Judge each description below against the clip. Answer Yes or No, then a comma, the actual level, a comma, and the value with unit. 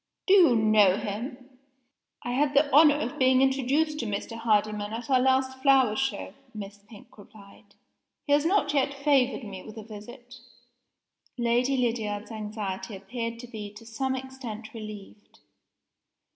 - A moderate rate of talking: Yes, average, 150 wpm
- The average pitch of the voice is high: Yes, high, 240 Hz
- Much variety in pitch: No, average, 3.9 semitones